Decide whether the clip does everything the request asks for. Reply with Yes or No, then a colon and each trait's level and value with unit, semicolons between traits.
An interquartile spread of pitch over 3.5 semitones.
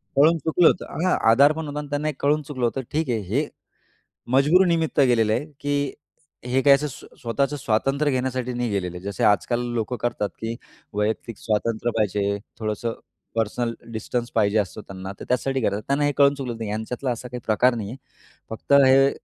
Yes: average, 4.4 semitones